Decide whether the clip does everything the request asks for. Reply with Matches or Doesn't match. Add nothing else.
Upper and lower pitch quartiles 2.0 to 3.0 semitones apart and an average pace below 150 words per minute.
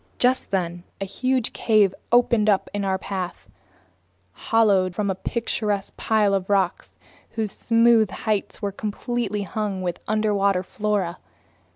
Matches